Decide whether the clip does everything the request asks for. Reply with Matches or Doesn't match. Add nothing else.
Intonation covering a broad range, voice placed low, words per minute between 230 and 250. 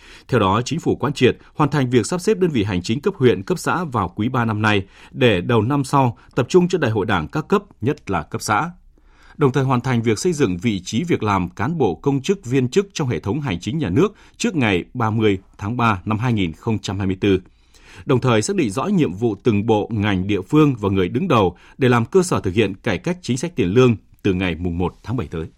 Matches